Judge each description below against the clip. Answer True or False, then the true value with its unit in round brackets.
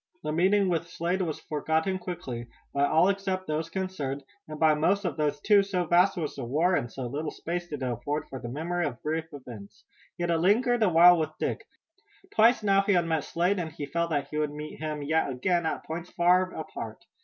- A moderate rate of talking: False (220 wpm)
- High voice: False (160 Hz)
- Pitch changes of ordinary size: True (3.6 semitones)